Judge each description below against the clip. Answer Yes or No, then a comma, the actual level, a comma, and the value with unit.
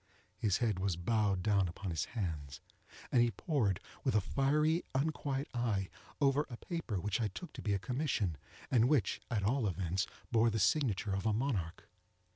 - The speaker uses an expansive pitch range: Yes, wide, 5.7 semitones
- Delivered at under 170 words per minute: No, average, 180 wpm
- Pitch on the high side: No, low, 110 Hz